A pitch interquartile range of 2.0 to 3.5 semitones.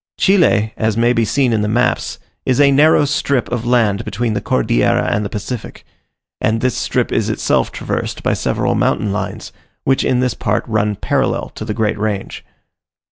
Yes: average, 3.1 semitones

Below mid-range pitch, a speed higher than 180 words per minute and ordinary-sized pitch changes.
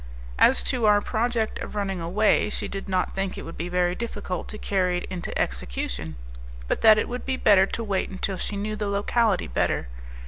No: high, 200 Hz; fast, 205 wpm; average, 3.0 semitones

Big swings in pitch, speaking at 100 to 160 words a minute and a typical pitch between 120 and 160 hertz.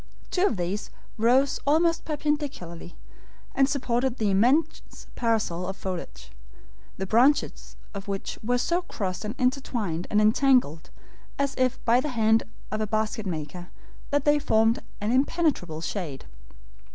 No: wide, 6.1 semitones; average, 140 wpm; high, 225 Hz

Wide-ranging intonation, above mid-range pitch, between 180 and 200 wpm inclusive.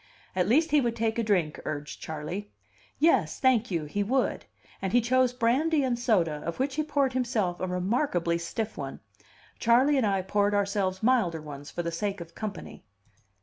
Yes: wide, 6.3 semitones; high, 205 Hz; average, 185 wpm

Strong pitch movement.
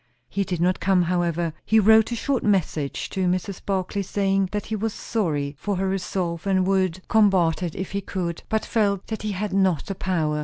No: narrow, 2.5 semitones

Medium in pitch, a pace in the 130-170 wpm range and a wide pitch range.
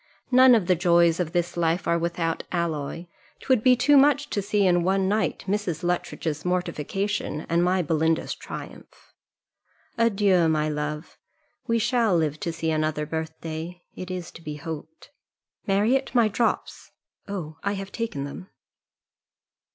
No: medium, 175 Hz; average, 150 wpm; average, 4.1 semitones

